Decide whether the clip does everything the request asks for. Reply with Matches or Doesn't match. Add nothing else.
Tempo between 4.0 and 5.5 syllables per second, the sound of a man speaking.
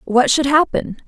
Doesn't match